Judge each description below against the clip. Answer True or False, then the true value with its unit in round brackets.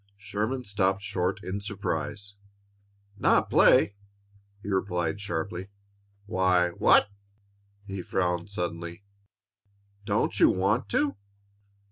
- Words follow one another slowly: True (100 wpm)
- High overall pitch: False (100 Hz)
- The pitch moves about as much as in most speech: False (2.3 semitones)